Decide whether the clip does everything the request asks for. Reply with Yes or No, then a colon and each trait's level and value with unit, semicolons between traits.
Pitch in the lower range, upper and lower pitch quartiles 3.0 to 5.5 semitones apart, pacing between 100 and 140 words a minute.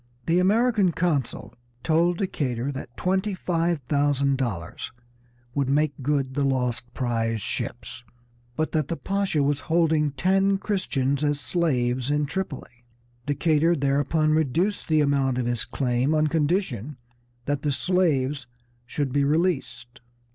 No: medium, 145 Hz; average, 4.2 semitones; slow, 135 wpm